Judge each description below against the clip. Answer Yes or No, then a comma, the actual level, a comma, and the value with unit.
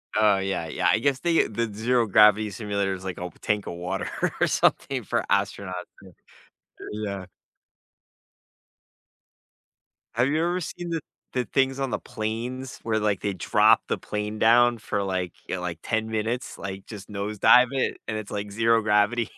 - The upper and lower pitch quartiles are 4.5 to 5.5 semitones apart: No, average, 3.5 semitones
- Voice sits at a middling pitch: No, low, 105 Hz